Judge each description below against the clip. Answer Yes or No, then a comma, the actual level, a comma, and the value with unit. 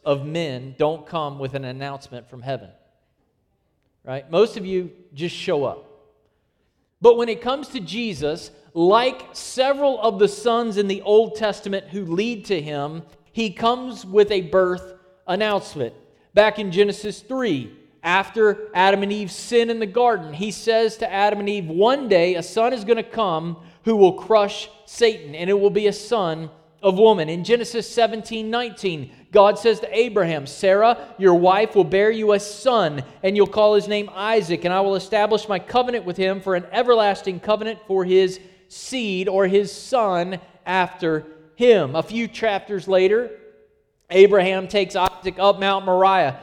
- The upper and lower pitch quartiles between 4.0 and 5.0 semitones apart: No, average, 3.6 semitones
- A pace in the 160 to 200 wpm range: Yes, average, 170 wpm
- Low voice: No, high, 200 Hz